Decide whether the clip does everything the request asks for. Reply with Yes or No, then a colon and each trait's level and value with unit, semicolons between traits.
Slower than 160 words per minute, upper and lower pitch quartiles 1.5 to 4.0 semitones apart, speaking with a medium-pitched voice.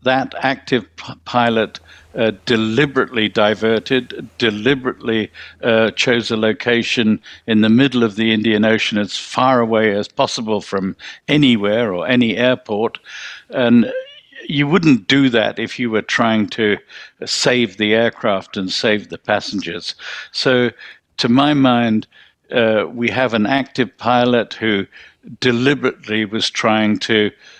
No: slow, 135 wpm; average, 2.8 semitones; low, 115 Hz